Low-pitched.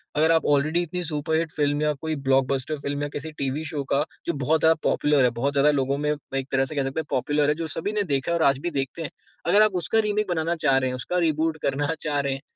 No: medium, 150 Hz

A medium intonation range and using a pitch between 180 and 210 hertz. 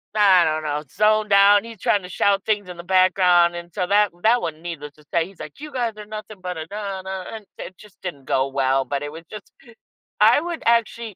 Yes: average, 4.0 semitones; high, 190 Hz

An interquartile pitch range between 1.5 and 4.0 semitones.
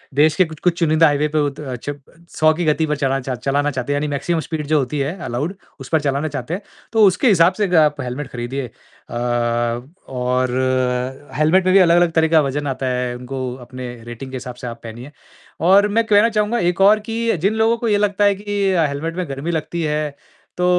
No: average, 5.3 semitones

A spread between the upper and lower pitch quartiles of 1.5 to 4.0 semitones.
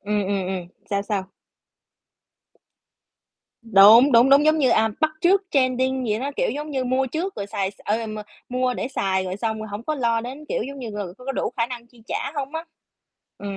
No: average, 4.7 semitones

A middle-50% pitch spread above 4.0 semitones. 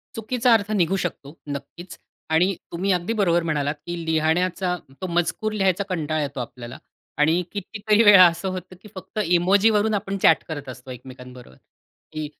Yes: average, 4.4 semitones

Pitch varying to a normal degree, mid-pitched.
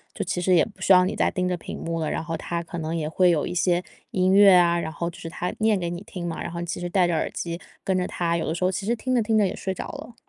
No: narrow, 1.9 semitones; medium, 175 Hz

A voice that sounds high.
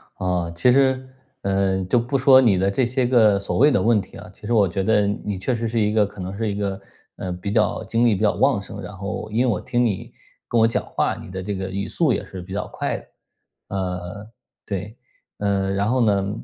No: low, 105 Hz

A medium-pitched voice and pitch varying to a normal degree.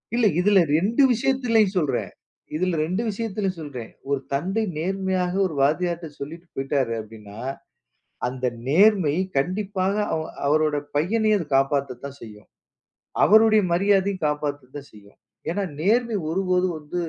No: medium, 170 Hz; wide, 5.9 semitones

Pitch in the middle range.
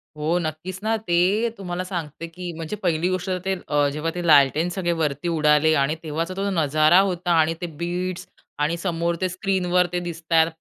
Yes: medium, 170 Hz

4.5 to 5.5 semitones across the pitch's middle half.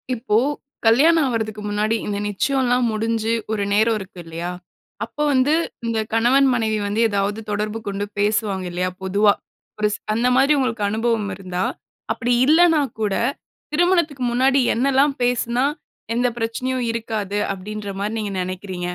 No: average, 3.6 semitones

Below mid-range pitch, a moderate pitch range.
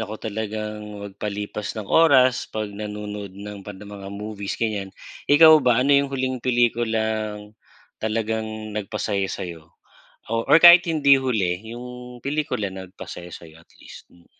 Yes: low, 110 Hz; average, 3.4 semitones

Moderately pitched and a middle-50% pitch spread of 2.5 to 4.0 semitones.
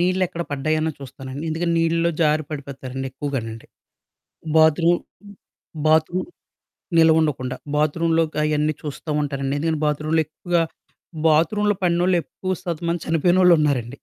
Yes: medium, 155 Hz; average, 2.8 semitones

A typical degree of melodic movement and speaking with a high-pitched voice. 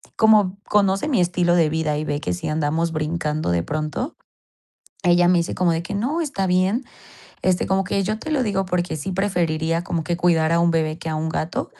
No: average, 3.4 semitones; medium, 175 Hz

